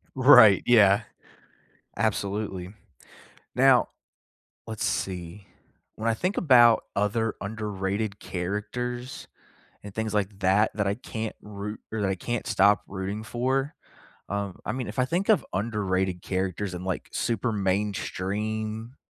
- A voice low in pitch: Yes, low, 105 Hz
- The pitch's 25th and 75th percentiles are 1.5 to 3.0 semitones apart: Yes, narrow, 2.6 semitones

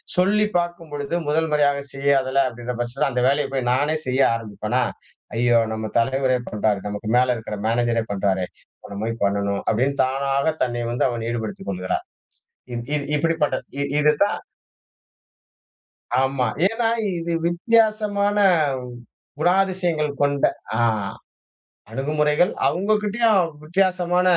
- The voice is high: No, medium, 140 Hz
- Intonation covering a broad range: Yes, wide, 6.5 semitones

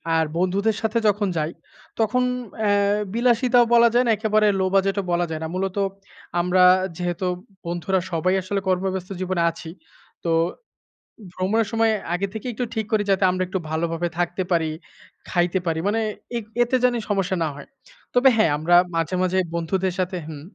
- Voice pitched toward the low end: No, high, 190 Hz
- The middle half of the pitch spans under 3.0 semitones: No, average, 3.8 semitones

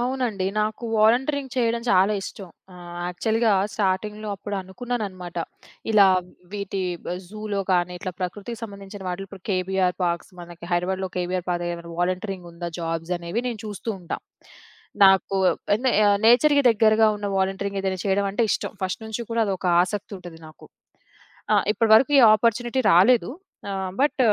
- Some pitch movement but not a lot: Yes, average, 3.4 semitones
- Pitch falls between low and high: No, high, 195 Hz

